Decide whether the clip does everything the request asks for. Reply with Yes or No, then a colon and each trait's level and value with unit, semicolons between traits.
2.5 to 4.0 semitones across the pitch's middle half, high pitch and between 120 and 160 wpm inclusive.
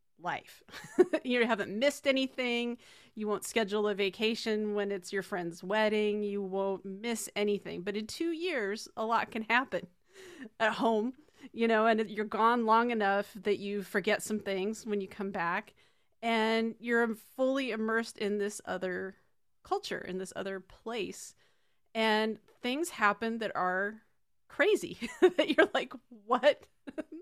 Yes: average, 3.1 semitones; high, 220 Hz; average, 150 wpm